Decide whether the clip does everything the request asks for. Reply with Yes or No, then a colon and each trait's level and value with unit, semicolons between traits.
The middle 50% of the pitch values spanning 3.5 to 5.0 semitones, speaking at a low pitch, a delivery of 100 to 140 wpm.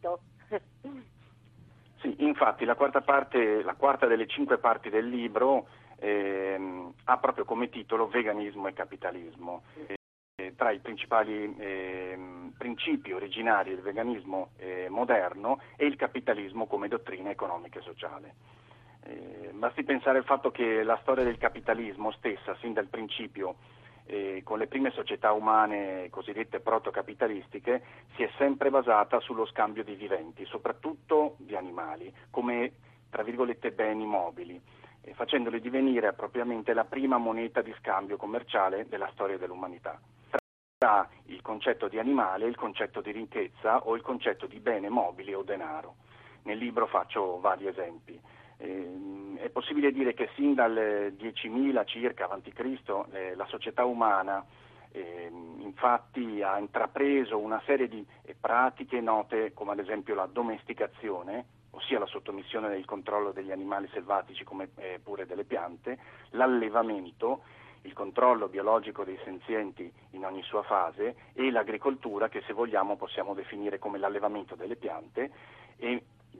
Yes: average, 4.0 semitones; low, 115 Hz; average, 135 wpm